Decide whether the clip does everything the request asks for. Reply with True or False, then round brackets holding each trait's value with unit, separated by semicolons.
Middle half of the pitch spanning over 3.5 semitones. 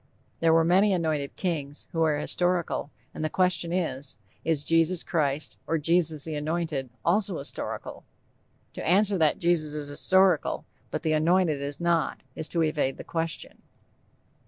False (2.7 semitones)